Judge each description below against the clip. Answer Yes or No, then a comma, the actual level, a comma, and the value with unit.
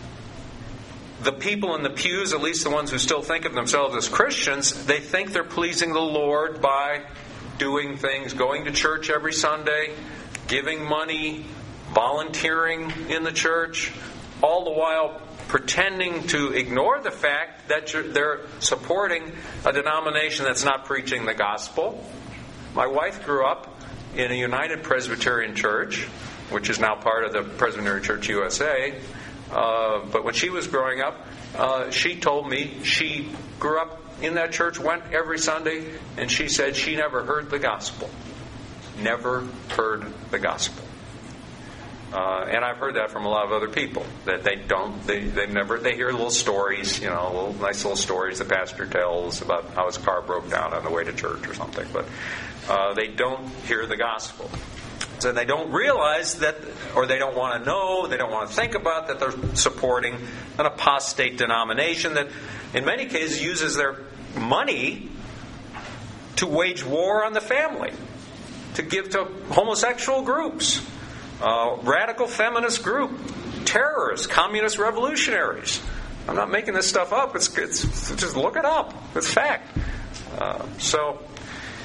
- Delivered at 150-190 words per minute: Yes, average, 160 wpm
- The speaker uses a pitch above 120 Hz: Yes, medium, 140 Hz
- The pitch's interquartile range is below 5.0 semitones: Yes, average, 4.6 semitones